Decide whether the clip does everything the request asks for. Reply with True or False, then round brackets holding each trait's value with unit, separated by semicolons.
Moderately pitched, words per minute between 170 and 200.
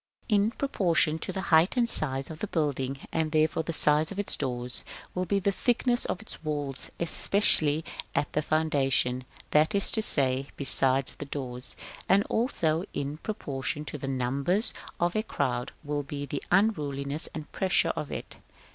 True (155 Hz; 175 wpm)